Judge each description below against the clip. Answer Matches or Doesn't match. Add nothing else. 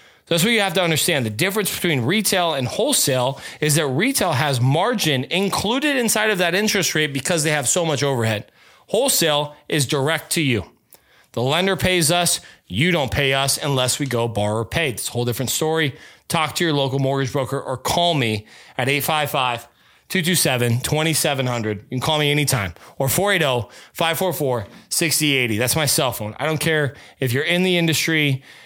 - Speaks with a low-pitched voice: Doesn't match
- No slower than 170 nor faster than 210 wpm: Matches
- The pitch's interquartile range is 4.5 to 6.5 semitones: Matches